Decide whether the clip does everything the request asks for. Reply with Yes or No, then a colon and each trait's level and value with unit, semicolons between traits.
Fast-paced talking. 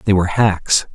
No: average, 190 wpm